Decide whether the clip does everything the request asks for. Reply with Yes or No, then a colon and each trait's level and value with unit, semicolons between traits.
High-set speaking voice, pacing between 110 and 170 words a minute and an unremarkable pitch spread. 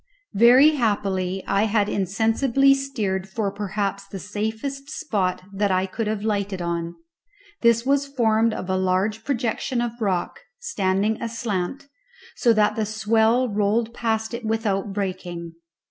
Yes: high, 215 Hz; average, 140 wpm; average, 3.2 semitones